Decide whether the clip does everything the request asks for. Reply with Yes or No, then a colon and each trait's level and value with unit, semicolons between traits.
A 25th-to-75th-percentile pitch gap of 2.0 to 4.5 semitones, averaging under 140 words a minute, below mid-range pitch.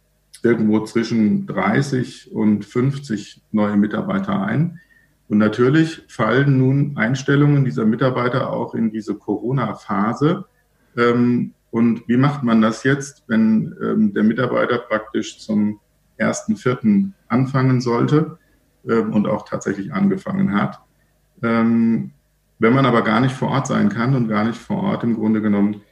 No: wide, 5.5 semitones; average, 130 wpm; low, 125 Hz